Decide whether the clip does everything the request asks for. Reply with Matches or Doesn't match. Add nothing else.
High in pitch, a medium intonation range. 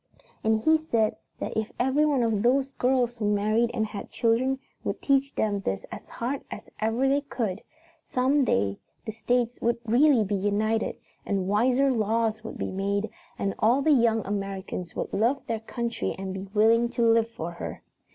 Matches